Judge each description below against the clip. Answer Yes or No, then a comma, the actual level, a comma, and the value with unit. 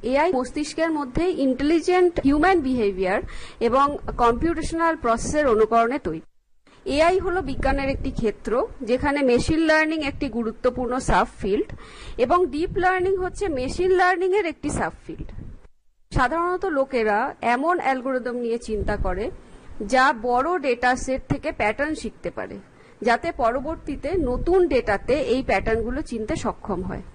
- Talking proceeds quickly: Yes, fast, 130 wpm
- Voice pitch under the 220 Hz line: No, very high, 275 Hz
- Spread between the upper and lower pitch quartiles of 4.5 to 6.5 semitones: Yes, wide, 5.5 semitones